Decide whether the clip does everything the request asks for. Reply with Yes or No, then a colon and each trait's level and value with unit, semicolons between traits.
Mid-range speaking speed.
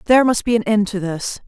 No: fast, 285 wpm